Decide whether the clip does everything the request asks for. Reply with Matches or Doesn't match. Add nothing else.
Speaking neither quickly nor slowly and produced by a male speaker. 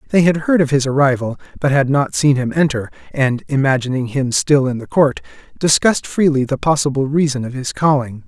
Matches